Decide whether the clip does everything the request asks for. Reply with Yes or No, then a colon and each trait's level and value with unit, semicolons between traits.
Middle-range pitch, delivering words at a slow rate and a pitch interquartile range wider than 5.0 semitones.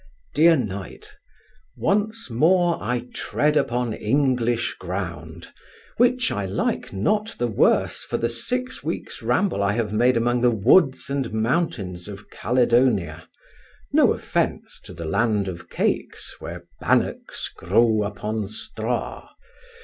No: low, 115 Hz; slow, 125 wpm; wide, 5.4 semitones